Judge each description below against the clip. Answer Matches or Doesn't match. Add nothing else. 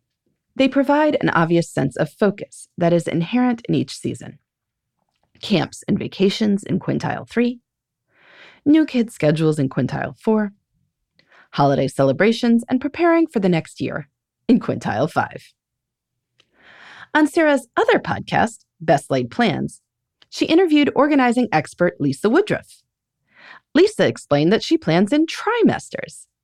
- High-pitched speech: Matches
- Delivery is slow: Matches